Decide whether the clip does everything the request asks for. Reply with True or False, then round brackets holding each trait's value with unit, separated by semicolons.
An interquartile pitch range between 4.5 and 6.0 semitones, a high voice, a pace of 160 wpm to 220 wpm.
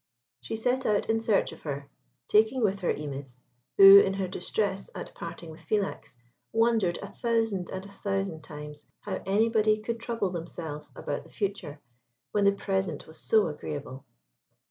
True (5.4 semitones; 195 Hz; 165 wpm)